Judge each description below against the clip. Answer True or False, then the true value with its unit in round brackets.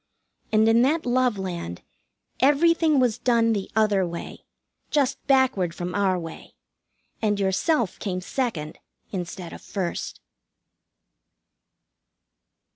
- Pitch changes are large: True (5.9 semitones)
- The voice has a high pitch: True (215 Hz)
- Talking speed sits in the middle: False (110 wpm)